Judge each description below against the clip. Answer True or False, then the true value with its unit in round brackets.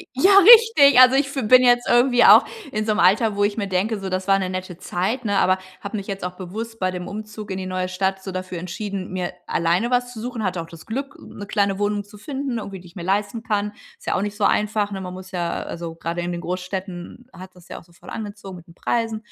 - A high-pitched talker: True (200 Hz)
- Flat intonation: False (3.5 semitones)